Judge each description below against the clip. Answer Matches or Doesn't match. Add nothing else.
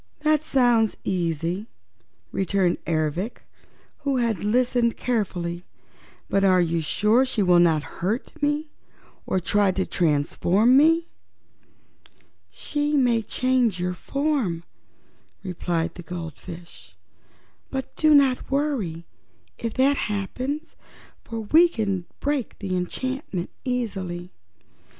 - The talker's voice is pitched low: Doesn't match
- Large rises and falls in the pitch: Matches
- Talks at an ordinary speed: Doesn't match